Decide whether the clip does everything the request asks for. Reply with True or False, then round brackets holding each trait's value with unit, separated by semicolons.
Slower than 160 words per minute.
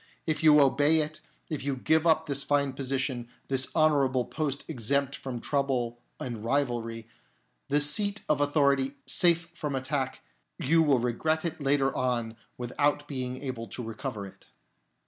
True (150 wpm)